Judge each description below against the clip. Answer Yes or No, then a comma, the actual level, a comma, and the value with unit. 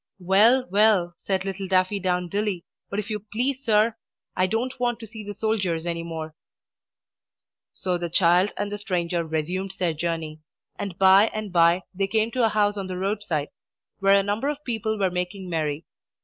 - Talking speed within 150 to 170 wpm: No, average, 180 wpm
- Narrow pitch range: No, average, 3.5 semitones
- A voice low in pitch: No, high, 195 Hz